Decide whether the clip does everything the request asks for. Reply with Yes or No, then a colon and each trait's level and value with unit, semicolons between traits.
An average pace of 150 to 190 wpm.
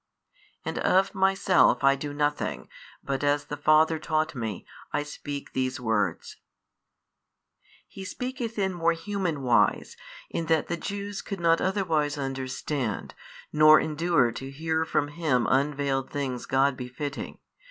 No: slow, 135 wpm